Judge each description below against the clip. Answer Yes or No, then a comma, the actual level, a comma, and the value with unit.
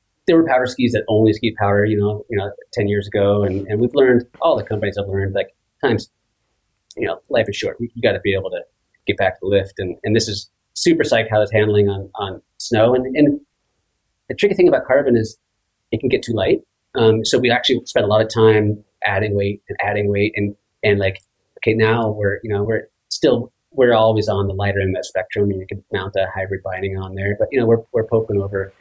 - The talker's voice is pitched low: Yes, low, 105 Hz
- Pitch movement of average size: No, narrow, 2.2 semitones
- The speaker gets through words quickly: Yes, fast, 245 wpm